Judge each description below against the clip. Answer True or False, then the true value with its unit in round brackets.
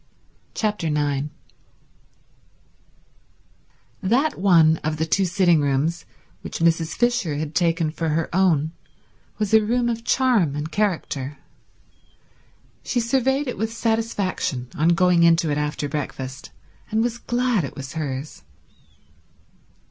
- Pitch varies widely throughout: True (6.7 semitones)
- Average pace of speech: False (125 wpm)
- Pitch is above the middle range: False (170 Hz)